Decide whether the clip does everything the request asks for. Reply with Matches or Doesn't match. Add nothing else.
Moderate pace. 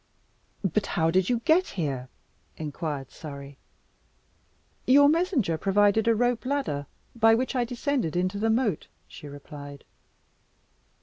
Doesn't match